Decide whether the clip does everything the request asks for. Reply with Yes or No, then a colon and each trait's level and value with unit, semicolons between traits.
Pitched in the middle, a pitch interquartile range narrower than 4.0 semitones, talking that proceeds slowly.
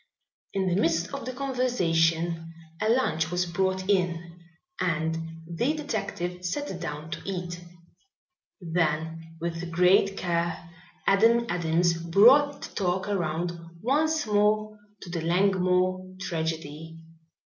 Yes: medium, 180 Hz; average, 3.5 semitones; slow, 115 wpm